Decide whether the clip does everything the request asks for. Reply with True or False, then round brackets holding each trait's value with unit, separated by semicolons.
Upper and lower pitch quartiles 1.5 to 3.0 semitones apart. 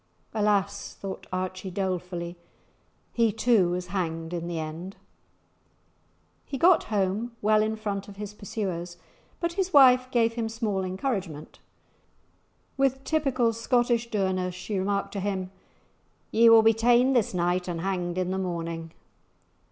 False (4.0 semitones)